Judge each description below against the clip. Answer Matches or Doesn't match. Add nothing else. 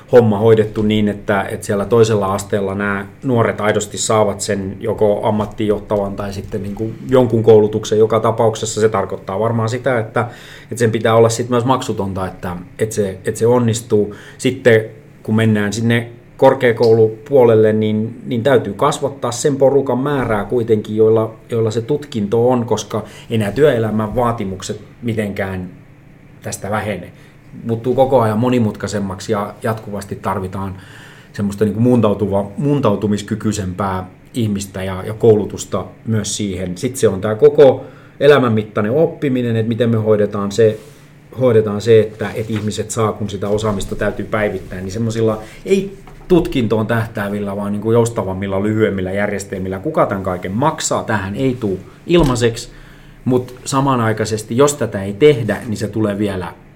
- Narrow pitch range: Doesn't match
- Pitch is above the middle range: Doesn't match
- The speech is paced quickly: Doesn't match